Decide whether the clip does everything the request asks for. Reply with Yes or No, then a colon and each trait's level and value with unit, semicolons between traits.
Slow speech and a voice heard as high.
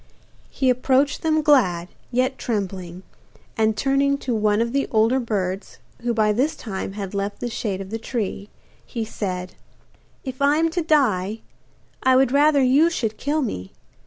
No: average, 165 wpm; high, 235 Hz